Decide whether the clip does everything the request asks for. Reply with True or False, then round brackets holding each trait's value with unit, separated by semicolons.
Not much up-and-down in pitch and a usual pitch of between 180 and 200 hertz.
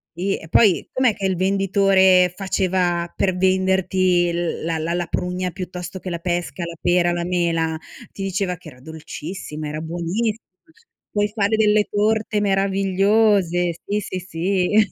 True (2.3 semitones; 185 Hz)